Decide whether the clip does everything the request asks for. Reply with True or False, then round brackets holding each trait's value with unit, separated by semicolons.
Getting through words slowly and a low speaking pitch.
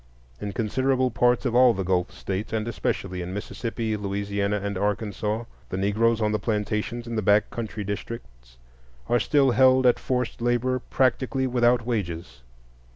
False (160 wpm; 110 Hz)